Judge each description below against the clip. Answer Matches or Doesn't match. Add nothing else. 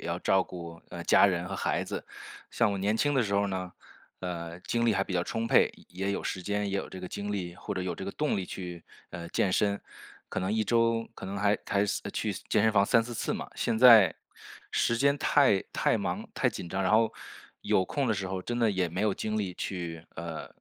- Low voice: Matches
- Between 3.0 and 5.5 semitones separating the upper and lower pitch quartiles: Matches